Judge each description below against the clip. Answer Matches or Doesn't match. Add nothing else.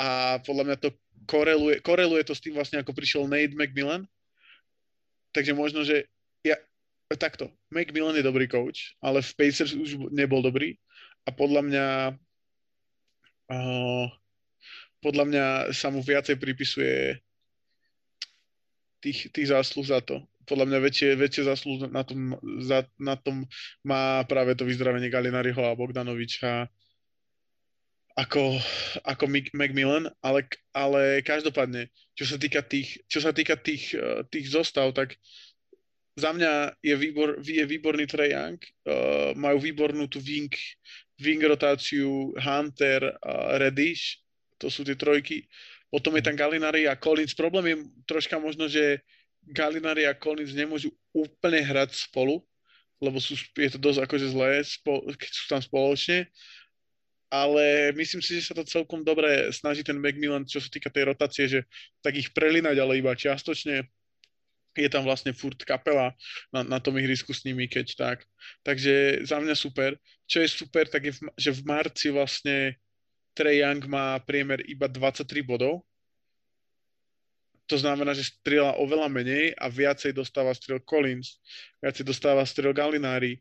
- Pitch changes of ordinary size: Doesn't match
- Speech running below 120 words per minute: Doesn't match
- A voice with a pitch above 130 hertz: Matches